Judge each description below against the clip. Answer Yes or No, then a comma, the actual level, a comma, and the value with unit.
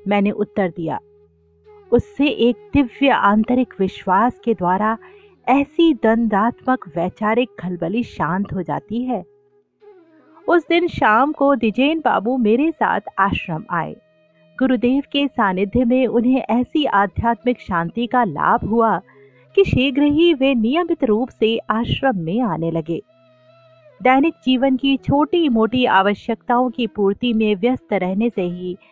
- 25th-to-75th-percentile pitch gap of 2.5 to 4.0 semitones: No, wide, 5.4 semitones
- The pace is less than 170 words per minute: Yes, average, 130 wpm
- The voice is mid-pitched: No, high, 235 Hz